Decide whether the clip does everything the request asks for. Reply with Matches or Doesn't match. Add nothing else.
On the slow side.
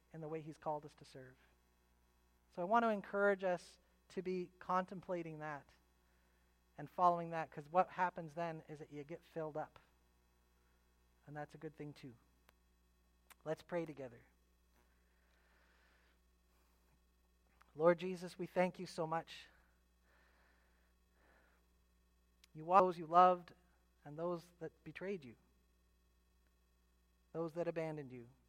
Matches